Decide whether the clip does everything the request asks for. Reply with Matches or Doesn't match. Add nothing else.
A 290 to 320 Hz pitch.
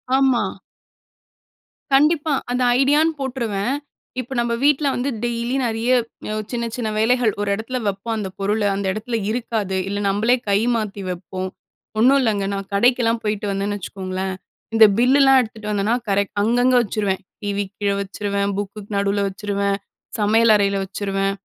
Doesn't match